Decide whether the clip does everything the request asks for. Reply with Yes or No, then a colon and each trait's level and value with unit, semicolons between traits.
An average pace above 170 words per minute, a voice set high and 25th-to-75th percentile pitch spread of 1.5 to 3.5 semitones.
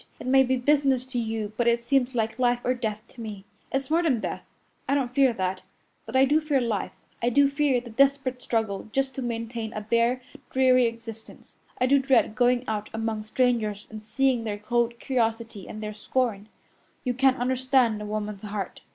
Yes: average, 195 wpm; high, 240 Hz; average, 3.0 semitones